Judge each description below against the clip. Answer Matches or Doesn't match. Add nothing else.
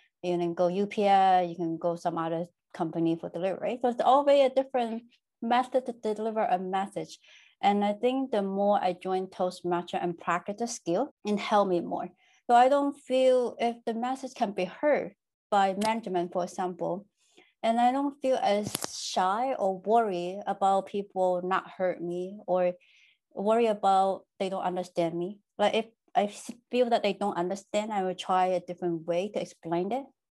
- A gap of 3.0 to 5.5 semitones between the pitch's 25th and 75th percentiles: Matches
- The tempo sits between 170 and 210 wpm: Matches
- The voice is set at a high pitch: Matches